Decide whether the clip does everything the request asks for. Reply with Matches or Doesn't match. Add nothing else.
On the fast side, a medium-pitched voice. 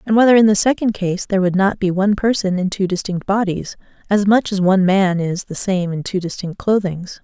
Doesn't match